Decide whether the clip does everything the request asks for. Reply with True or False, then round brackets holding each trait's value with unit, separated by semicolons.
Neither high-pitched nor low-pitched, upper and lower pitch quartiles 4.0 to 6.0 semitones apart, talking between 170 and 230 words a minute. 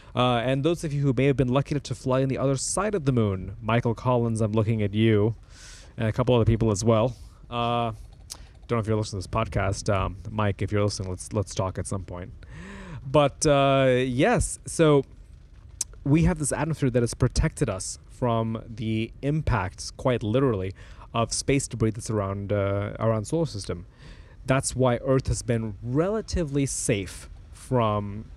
False (115 Hz; 4.9 semitones; 185 wpm)